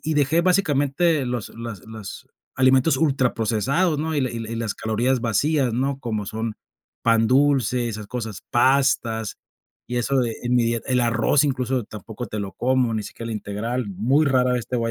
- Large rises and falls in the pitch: No, average, 3.2 semitones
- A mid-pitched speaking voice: No, low, 125 Hz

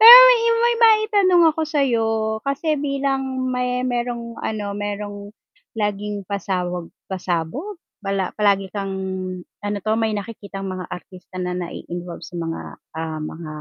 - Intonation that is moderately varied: No, wide, 6.5 semitones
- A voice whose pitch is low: No, high, 205 Hz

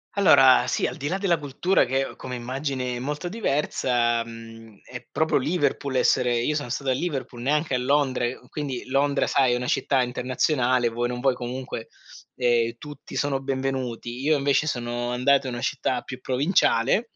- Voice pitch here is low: Yes, low, 130 Hz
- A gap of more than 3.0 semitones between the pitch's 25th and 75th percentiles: No, average, 2.7 semitones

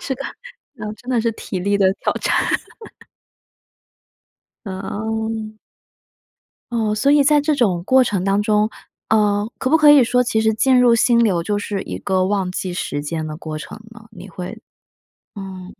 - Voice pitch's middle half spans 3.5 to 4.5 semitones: Yes, average, 3.9 semitones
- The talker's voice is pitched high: Yes, high, 210 Hz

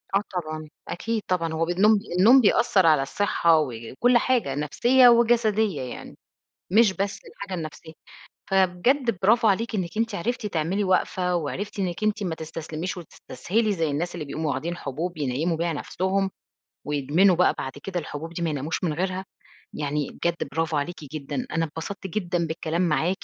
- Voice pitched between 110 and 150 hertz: No, medium, 175 Hz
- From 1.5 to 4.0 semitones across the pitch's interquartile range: No, average, 4.4 semitones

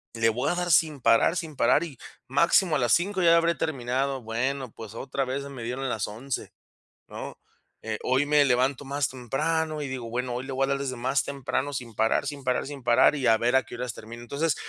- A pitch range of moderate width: Yes, average, 3.0 semitones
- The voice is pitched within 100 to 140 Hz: Yes, low, 135 Hz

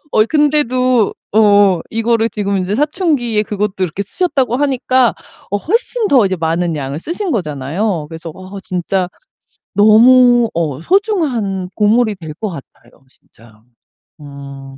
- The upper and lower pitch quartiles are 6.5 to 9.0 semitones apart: Yes, wide, 6.8 semitones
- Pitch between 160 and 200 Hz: No, high, 210 Hz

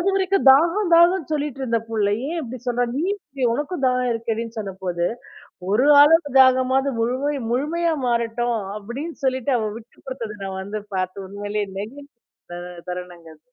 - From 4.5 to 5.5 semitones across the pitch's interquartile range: Yes, average, 5.2 semitones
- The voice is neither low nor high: No, very high, 250 Hz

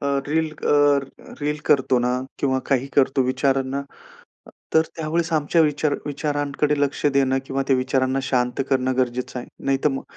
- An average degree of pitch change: No, narrow, 2.1 semitones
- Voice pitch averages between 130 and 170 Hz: Yes, low, 135 Hz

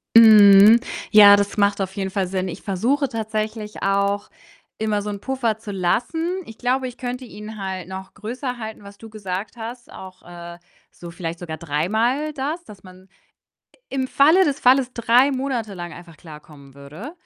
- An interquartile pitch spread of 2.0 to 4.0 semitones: No, average, 4.7 semitones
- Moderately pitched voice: No, high, 210 Hz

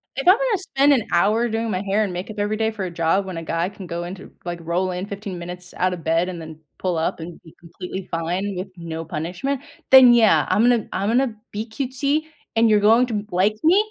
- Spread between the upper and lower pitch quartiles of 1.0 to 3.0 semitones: No, average, 4.6 semitones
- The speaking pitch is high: Yes, high, 195 Hz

